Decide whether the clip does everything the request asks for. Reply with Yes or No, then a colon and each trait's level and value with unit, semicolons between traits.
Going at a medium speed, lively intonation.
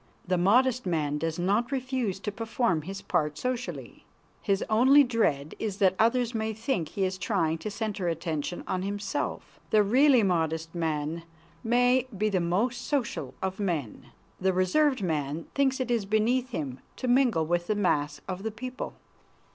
Yes: average, 165 wpm; wide, 6.1 semitones